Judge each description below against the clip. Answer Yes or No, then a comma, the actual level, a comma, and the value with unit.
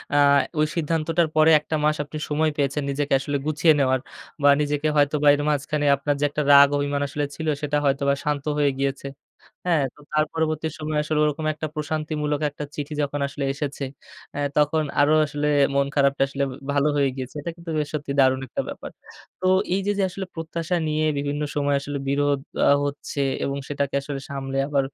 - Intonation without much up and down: Yes, narrow, 1.5 semitones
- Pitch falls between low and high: Yes, medium, 145 Hz